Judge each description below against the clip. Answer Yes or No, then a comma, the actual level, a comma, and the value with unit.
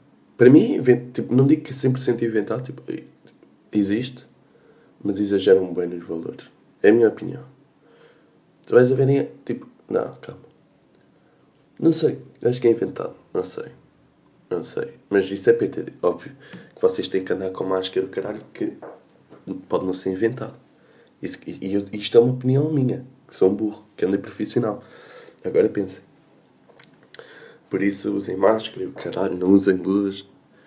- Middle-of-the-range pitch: No, low, 115 Hz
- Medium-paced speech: Yes, average, 165 wpm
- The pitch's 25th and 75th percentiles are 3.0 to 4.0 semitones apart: No, average, 5.3 semitones